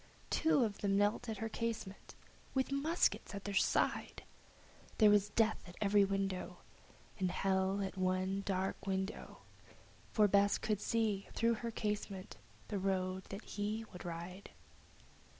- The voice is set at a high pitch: Yes, high, 200 Hz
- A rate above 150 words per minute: No, average, 145 wpm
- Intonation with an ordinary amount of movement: No, narrow, 2.2 semitones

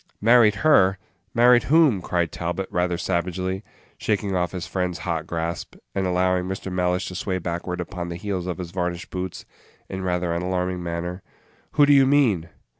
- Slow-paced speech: No, average, 175 wpm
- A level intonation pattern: Yes, narrow, 1.8 semitones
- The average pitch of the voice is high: No, very low, 90 Hz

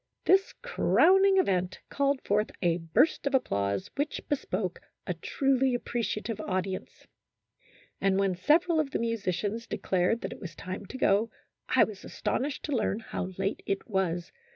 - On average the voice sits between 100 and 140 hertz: No, high, 210 Hz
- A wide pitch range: Yes, wide, 6.7 semitones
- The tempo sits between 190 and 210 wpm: No, average, 160 wpm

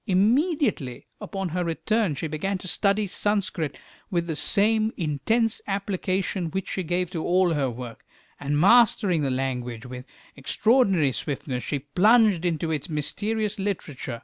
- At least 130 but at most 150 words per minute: Yes, average, 145 wpm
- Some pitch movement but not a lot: No, wide, 5.8 semitones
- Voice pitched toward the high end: No, medium, 180 Hz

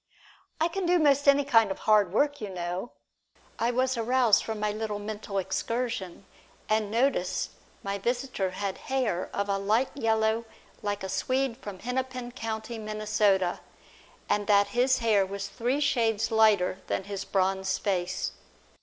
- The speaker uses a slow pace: No, average, 155 wpm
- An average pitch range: Yes, average, 4.0 semitones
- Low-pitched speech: No, high, 220 Hz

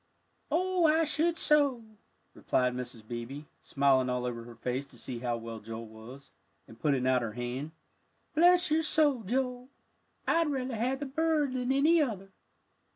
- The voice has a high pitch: Yes, high, 195 Hz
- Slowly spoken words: No, average, 160 wpm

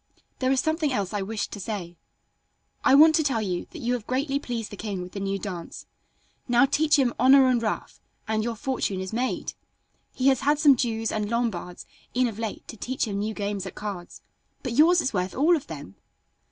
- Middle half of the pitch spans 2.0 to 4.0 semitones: No, average, 4.9 semitones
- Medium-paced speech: No, fast, 215 wpm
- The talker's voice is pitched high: Yes, high, 230 Hz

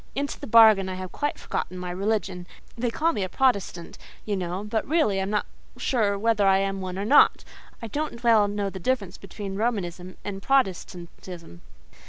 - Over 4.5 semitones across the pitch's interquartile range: No, average, 3.5 semitones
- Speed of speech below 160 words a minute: No, average, 190 wpm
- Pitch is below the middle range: No, high, 200 Hz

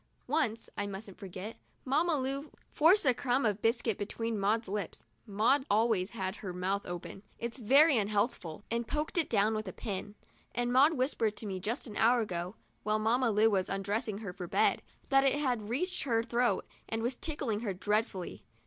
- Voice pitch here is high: Yes, high, 225 Hz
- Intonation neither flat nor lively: Yes, average, 4.0 semitones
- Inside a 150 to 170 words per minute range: No, average, 190 wpm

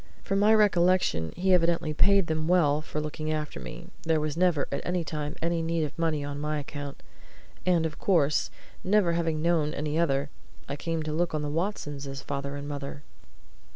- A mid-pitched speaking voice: Yes, medium, 155 Hz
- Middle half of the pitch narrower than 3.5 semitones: Yes, average, 2.8 semitones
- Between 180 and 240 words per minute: Yes, average, 190 wpm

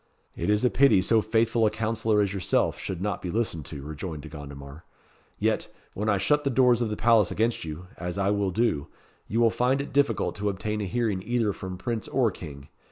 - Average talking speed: No, fast, 220 wpm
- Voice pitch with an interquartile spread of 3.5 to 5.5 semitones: Yes, average, 4.5 semitones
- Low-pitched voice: Yes, low, 105 Hz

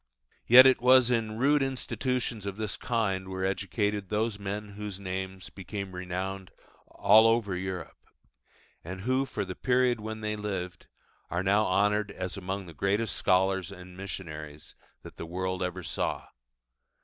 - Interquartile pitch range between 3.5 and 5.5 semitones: No, average, 2.8 semitones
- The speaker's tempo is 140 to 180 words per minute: Yes, average, 155 wpm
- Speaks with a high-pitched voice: No, low, 100 Hz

